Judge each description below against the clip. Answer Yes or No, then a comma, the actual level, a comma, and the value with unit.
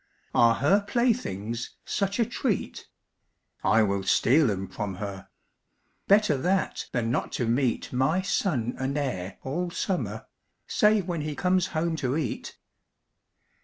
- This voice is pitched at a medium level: Yes, medium, 145 Hz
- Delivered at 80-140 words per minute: Yes, slow, 135 wpm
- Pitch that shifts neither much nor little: No, wide, 8.4 semitones